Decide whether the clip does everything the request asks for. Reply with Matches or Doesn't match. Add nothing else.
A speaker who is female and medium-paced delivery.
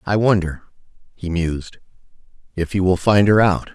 Doesn't match